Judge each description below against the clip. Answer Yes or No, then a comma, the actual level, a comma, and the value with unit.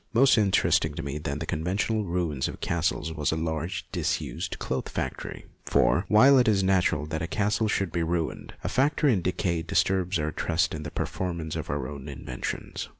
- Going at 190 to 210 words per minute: Yes, average, 195 wpm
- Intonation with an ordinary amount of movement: Yes, average, 4.1 semitones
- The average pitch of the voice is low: Yes, very low, 85 Hz